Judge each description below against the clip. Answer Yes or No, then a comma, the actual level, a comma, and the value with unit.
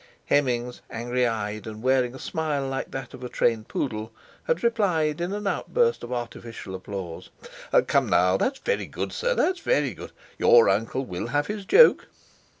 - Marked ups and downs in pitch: Yes, wide, 7.3 semitones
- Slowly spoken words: No, average, 160 wpm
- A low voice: Yes, low, 130 Hz